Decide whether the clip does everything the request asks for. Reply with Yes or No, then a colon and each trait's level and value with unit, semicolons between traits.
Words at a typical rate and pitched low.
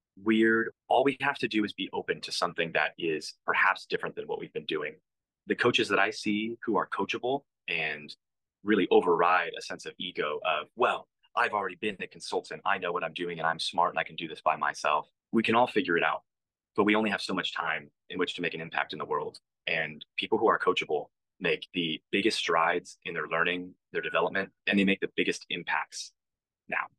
No: fast, 220 wpm; low, 110 Hz